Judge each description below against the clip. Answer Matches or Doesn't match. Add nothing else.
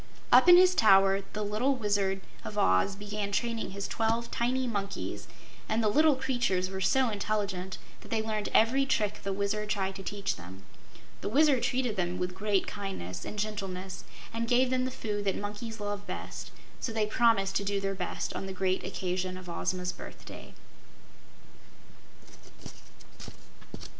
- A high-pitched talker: Matches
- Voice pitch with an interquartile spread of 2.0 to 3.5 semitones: Matches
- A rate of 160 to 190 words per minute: Matches